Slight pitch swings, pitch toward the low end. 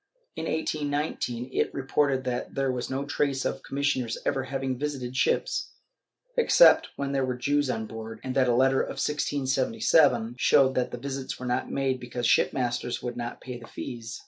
Yes: narrow, 2.3 semitones; low, 130 Hz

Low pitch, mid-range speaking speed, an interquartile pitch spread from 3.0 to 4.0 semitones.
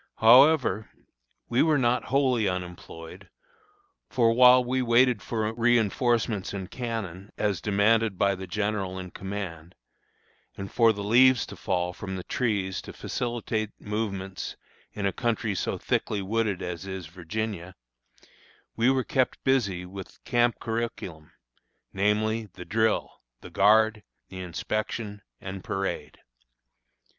No: low, 105 Hz; slow, 130 wpm; average, 3.6 semitones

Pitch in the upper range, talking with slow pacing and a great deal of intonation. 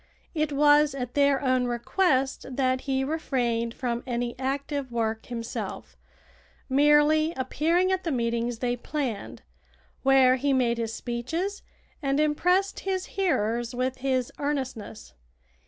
No: very high, 265 Hz; slow, 125 wpm; average, 3.7 semitones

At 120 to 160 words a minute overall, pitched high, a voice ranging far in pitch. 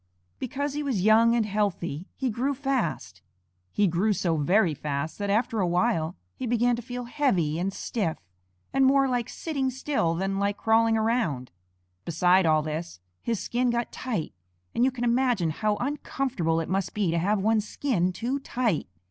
No: average, 175 wpm; high, 215 Hz; wide, 6.1 semitones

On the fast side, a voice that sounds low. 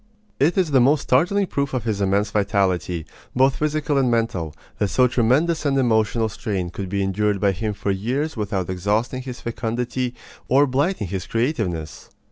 No: average, 170 wpm; low, 115 Hz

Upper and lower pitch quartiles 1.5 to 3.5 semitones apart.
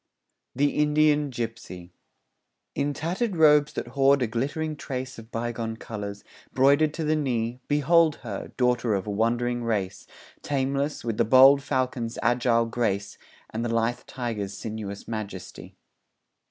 No: average, 4.0 semitones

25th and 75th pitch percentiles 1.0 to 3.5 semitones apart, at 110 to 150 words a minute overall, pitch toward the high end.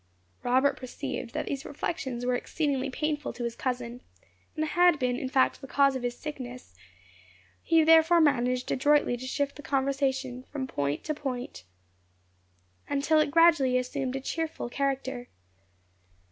Yes: average, 2.8 semitones; average, 145 wpm; very high, 270 Hz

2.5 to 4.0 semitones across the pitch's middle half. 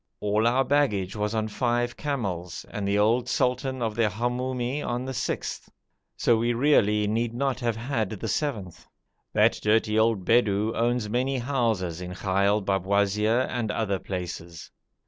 Yes: average, 3.3 semitones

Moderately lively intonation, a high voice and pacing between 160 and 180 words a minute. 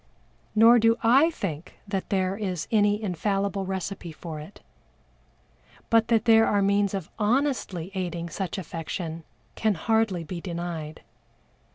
No: average, 4.1 semitones; high, 195 Hz; slow, 135 wpm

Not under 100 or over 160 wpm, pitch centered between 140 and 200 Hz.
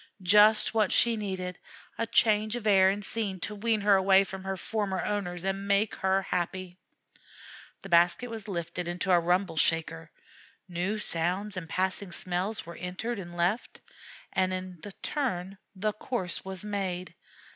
Yes: average, 155 wpm; high, 190 Hz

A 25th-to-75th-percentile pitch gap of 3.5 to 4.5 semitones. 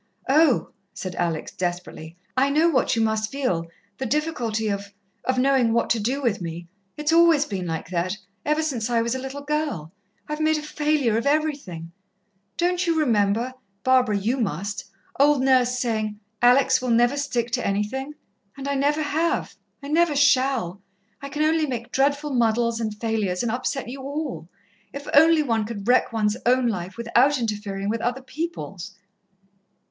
No: average, 5.1 semitones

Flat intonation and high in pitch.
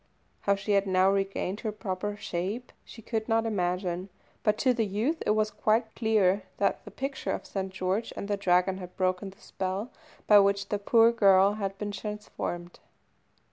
Yes: narrow, 2.3 semitones; high, 200 Hz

